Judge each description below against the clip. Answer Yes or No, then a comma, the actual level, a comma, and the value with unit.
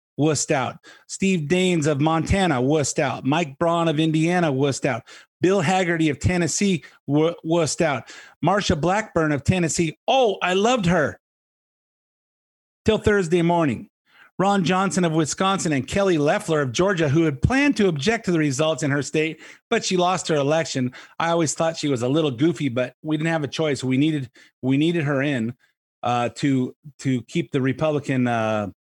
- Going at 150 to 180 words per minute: Yes, average, 175 wpm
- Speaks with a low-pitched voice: No, medium, 160 Hz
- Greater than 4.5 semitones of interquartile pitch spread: No, average, 3.8 semitones